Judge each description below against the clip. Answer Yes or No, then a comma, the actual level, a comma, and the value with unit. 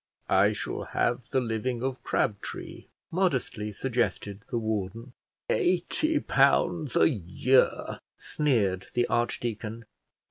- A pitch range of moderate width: Yes, average, 3.9 semitones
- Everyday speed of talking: No, slow, 105 wpm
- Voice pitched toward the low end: Yes, low, 120 Hz